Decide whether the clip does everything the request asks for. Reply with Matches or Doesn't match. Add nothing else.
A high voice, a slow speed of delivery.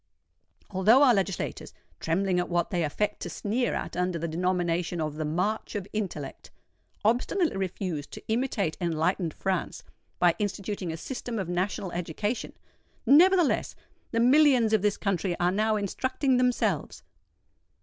Matches